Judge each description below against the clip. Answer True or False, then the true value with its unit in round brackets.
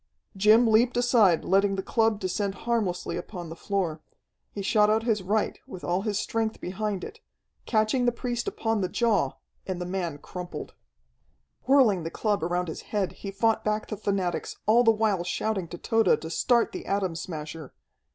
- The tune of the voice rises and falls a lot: False (3.7 semitones)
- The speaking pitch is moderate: False (200 Hz)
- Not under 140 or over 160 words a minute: False (180 wpm)